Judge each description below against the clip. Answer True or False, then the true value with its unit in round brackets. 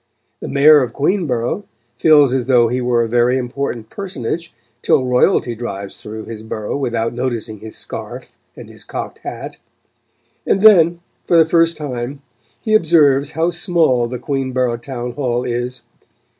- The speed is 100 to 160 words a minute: True (155 wpm)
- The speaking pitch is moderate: False (130 Hz)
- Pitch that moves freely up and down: False (4.5 semitones)